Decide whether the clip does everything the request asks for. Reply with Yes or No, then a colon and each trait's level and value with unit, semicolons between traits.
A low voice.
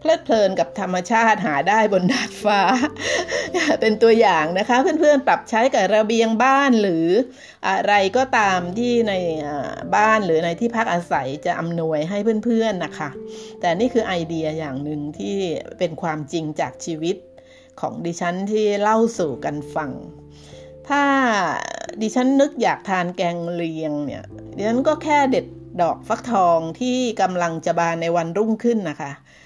No: high, 195 Hz